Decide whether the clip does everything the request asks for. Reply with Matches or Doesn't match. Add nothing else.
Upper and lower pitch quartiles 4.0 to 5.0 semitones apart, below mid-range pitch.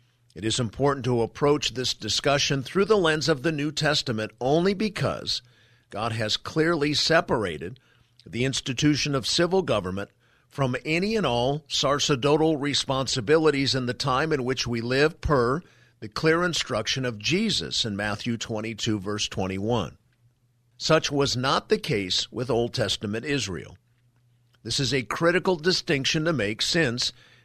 Matches